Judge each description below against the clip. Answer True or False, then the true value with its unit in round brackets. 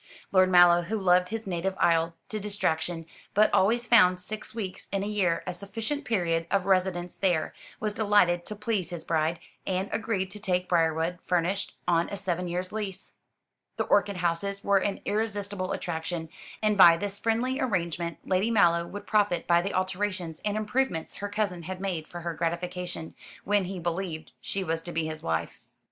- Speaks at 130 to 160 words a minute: False (180 wpm)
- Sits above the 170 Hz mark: True (185 Hz)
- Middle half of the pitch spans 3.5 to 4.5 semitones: False (3.0 semitones)